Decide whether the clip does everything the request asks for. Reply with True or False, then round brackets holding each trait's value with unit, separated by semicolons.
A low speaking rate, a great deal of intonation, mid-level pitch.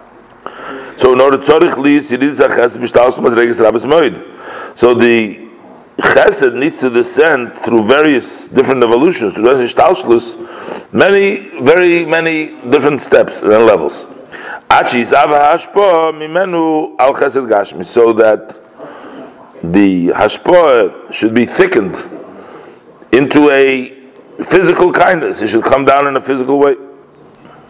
True (90 wpm; 7.8 semitones; 145 Hz)